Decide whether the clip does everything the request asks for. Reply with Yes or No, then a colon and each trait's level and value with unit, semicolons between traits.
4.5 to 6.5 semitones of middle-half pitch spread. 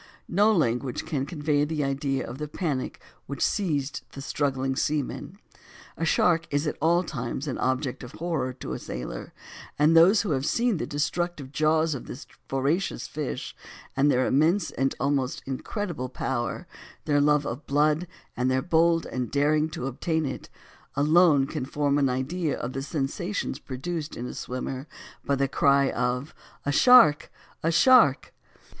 No: average, 3.4 semitones